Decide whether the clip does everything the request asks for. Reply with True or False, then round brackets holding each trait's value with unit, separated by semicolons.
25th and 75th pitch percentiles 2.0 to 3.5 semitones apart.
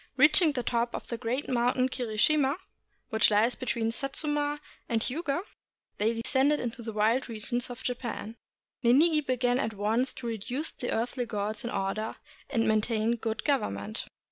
True (3.2 semitones)